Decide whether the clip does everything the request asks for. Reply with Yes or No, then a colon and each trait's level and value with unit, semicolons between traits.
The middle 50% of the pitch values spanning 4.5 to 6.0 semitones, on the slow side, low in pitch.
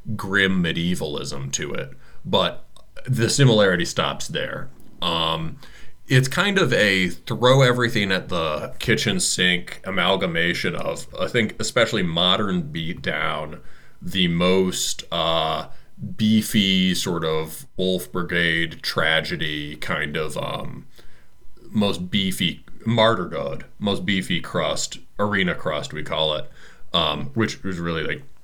Yes: average, 5.1 semitones; slow, 120 wpm; very low, 95 Hz